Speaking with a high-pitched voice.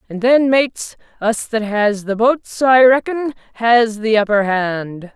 Yes: high, 230 Hz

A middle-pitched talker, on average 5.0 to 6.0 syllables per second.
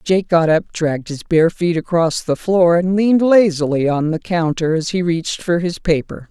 No: medium, 170 Hz; 4.8 syllables/s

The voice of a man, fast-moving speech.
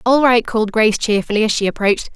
No: female; fast, 225 wpm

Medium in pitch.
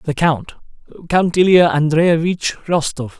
Yes: medium, 160 Hz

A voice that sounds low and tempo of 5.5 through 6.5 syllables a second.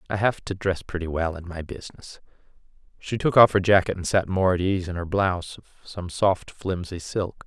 No: very low, 90 Hz; 5.3 syllables/s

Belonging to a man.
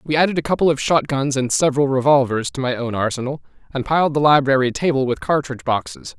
Yes: male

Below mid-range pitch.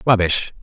Yes: low, 100 Hz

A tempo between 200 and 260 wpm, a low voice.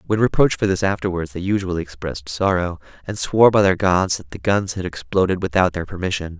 Yes: fast, 205 wpm; very low, 90 Hz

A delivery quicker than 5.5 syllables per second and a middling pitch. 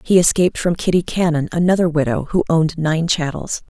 Yes: 5.9 syllables/s; medium, 165 Hz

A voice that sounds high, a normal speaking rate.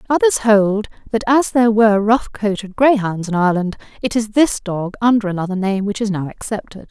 Yes: high, 210 Hz; average, 190 wpm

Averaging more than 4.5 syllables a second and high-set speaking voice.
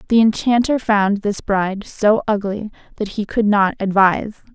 Yes: 4.7 syllables/s; high, 210 Hz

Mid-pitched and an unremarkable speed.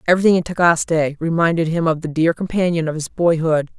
Yes: medium, 165 Hz; average, 190 wpm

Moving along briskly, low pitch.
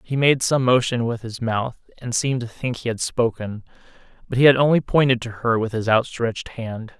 Yes: fast, 215 wpm; low, 120 Hz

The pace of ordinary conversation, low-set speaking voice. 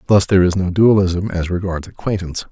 Yes: average, 190 wpm; very low, 95 Hz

